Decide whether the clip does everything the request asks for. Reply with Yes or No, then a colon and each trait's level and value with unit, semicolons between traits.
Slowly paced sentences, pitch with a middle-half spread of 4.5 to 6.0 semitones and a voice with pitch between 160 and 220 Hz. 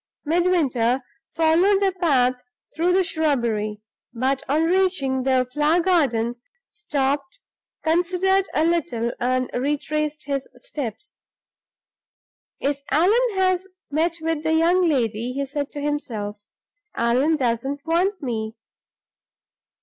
No: slow, 110 wpm; average, 5.2 semitones; very high, 295 Hz